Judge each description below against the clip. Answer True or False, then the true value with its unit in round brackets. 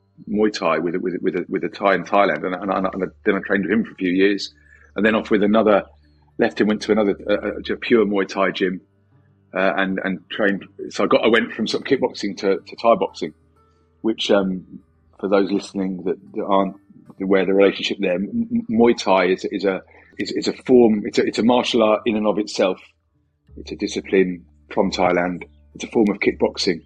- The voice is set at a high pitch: False (95 Hz)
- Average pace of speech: False (220 wpm)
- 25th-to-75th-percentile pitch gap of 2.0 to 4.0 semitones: True (2.5 semitones)